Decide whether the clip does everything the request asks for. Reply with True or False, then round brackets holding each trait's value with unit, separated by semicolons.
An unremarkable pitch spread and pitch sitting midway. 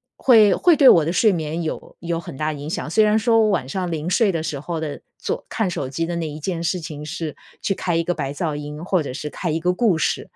True (3.6 semitones; 165 Hz)